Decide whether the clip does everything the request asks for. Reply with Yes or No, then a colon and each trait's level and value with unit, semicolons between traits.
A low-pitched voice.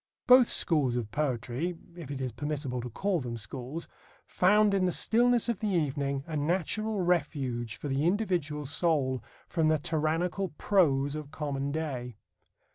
No: medium, 150 Hz